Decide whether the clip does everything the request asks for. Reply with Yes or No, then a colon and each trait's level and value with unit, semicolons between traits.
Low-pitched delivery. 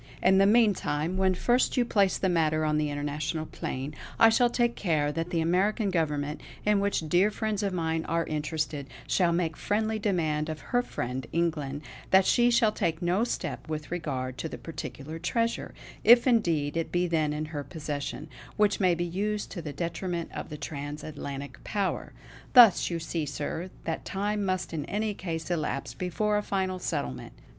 No: medium, 170 Hz